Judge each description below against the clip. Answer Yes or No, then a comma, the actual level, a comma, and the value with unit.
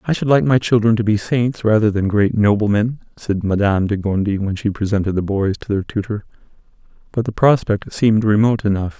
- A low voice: Yes, low, 105 Hz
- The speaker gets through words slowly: No, average, 200 wpm